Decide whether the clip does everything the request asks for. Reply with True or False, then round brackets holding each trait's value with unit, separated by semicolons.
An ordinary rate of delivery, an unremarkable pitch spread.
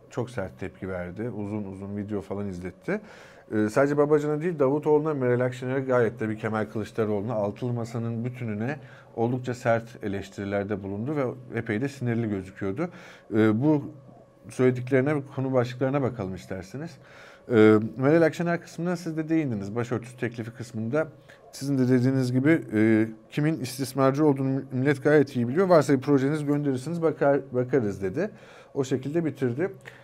False (145 wpm; 4.5 semitones)